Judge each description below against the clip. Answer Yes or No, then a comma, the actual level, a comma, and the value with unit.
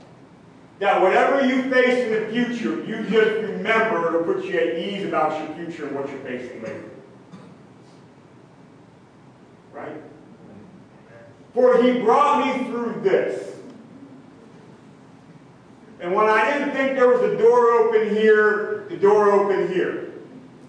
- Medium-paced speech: No, slow, 130 wpm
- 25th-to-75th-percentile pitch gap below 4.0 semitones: No, average, 5.0 semitones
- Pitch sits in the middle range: No, high, 220 Hz